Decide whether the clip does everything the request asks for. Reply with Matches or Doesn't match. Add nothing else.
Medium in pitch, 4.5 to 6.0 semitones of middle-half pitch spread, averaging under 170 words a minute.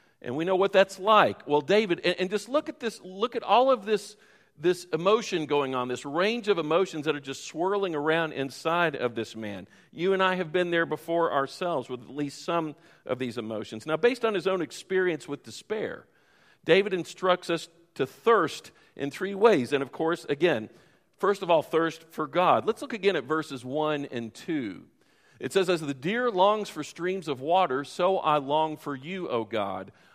Doesn't match